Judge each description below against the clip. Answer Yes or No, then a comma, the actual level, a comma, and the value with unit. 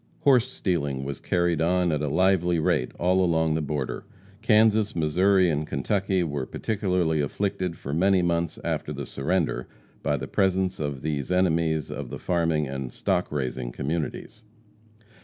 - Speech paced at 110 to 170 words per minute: Yes, average, 155 wpm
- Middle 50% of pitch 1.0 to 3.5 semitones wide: No, average, 4.0 semitones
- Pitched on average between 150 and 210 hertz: No, very low, 85 Hz